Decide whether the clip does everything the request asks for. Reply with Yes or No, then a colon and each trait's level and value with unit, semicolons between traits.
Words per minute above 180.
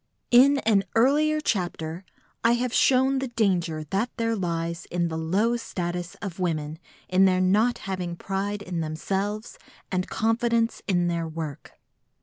No: average, 145 wpm